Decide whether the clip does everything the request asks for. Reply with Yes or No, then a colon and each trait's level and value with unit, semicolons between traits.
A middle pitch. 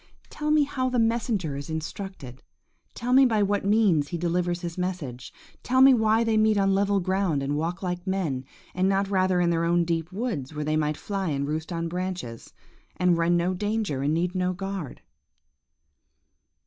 Yes: medium, 180 Hz